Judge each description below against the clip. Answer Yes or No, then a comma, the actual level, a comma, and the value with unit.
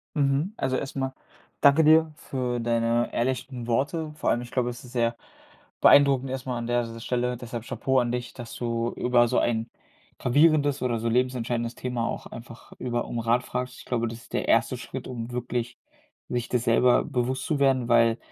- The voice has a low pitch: Yes, low, 125 Hz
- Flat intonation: Yes, narrow, 1.9 semitones